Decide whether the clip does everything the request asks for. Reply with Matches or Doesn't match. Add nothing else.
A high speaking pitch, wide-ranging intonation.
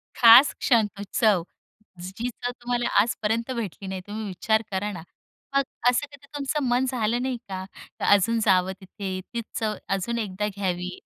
Doesn't match